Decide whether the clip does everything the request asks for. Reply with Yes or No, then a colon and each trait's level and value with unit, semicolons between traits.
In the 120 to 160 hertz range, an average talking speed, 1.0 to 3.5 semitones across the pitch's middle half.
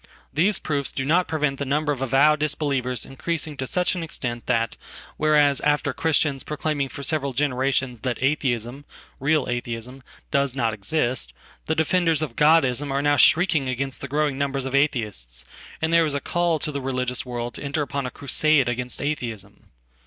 Yes: medium, 140 Hz; average, 165 wpm; average, 3.2 semitones